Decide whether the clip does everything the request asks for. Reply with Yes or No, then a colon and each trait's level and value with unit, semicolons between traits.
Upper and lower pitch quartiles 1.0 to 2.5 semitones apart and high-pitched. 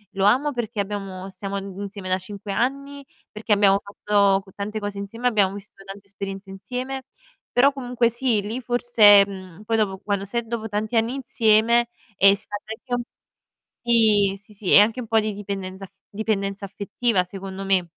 No: average, 2.9 semitones; high, 205 Hz